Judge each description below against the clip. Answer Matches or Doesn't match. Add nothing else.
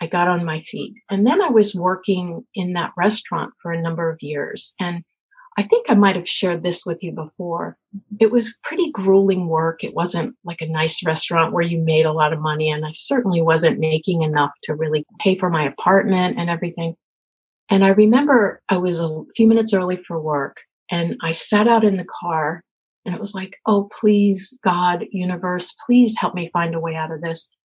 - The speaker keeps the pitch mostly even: Doesn't match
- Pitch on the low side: Doesn't match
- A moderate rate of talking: Doesn't match